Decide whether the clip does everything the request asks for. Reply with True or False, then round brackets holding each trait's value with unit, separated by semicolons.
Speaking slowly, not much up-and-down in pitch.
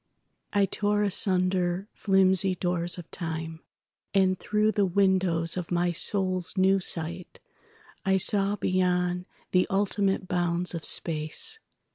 True (110 wpm; 1.9 semitones)